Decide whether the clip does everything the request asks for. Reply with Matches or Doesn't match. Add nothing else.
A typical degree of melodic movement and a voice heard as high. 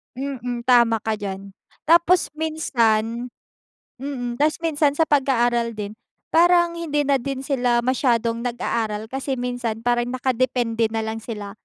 Matches